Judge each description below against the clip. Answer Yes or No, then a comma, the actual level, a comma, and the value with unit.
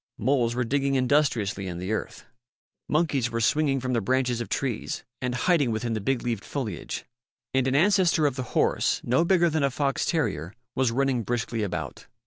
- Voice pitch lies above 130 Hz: No, low, 125 Hz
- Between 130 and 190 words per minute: Yes, average, 185 wpm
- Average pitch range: Yes, average, 3.6 semitones